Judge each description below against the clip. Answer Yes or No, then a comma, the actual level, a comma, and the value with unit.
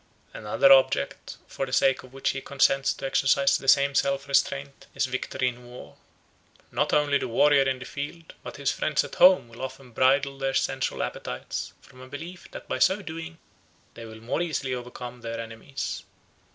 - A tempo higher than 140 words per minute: Yes, average, 190 wpm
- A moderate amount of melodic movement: No, narrow, 2.0 semitones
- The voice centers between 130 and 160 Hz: Yes, low, 135 Hz